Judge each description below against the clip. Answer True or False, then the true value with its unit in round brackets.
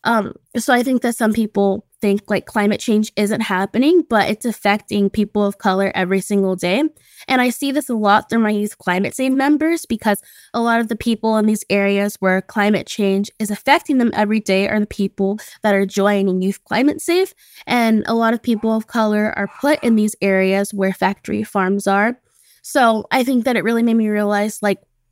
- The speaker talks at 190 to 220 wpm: True (205 wpm)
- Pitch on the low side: False (215 Hz)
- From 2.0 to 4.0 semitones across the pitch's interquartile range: True (2.7 semitones)